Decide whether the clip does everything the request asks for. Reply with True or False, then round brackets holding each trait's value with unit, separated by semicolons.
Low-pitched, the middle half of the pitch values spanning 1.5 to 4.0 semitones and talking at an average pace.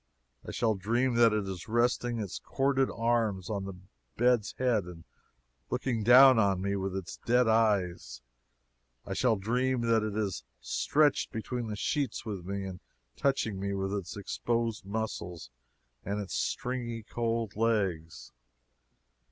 True (110 Hz; 3.5 semitones; 145 wpm)